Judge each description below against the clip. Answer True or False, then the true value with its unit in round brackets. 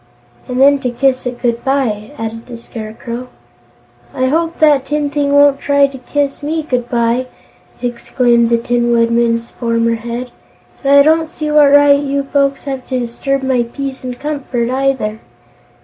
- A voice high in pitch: True (260 Hz)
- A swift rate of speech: False (165 wpm)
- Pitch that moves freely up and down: False (3.1 semitones)